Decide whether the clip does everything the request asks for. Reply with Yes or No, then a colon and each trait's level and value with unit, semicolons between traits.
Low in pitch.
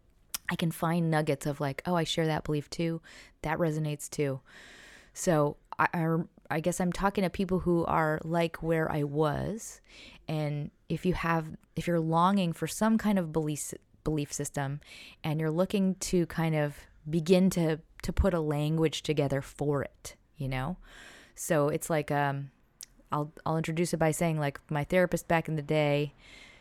No: medium, 160 Hz